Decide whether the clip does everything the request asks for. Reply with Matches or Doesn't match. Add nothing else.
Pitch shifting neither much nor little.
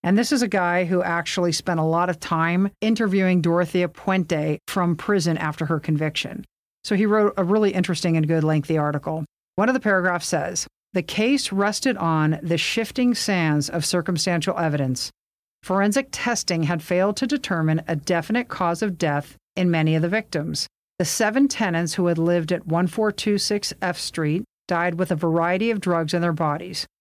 Matches